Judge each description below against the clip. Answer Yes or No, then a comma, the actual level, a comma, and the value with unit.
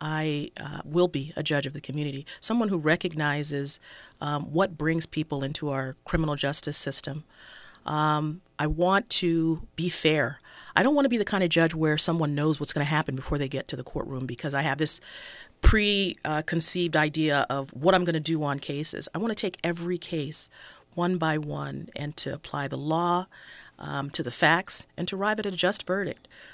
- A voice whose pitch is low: No, medium, 155 Hz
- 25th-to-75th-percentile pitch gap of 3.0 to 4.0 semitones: Yes, average, 3.4 semitones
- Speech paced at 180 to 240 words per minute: Yes, average, 200 wpm